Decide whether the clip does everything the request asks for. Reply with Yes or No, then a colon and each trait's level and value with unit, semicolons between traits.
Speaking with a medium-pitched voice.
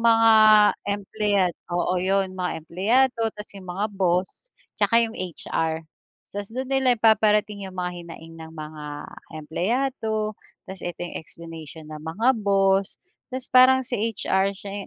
No: high, 195 Hz